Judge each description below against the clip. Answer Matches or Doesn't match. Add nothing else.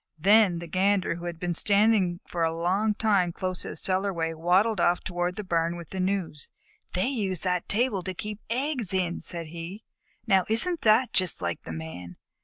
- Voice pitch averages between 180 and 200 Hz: Matches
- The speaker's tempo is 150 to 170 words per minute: Doesn't match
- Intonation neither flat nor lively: Matches